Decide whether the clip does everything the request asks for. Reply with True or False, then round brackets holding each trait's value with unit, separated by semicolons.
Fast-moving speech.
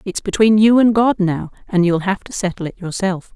True (230 wpm)